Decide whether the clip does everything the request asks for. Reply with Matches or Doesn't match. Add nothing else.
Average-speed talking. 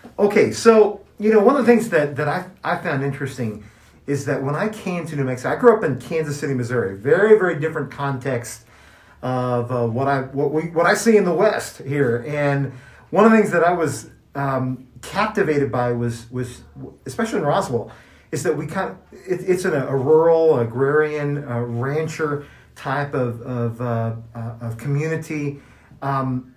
Matches